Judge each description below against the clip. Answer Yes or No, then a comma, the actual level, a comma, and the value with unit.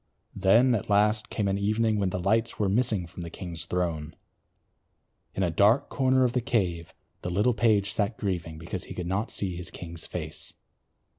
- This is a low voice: Yes, low, 100 Hz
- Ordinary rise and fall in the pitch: Yes, average, 4.0 semitones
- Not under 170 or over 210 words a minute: Yes, average, 190 wpm